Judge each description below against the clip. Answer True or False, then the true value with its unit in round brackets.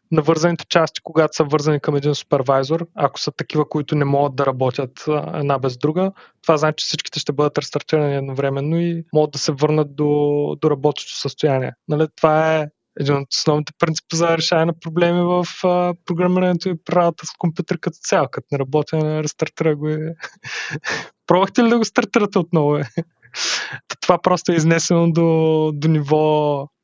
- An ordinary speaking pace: False (170 wpm)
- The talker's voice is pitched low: False (155 Hz)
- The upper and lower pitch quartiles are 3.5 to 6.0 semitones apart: False (2.5 semitones)